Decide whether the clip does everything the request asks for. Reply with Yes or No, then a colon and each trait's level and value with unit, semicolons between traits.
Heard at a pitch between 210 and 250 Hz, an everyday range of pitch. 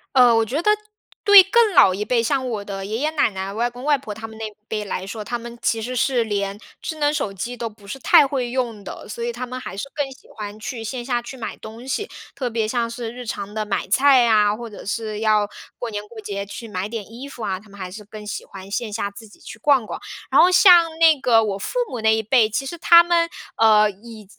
Yes: high, 230 Hz; average, 3.5 semitones